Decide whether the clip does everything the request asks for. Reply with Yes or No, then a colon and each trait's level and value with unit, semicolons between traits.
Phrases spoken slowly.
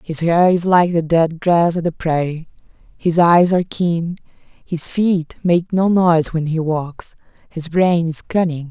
No: average, 180 wpm